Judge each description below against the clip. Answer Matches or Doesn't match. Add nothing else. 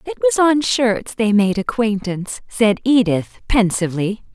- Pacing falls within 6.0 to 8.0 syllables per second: Doesn't match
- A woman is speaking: Matches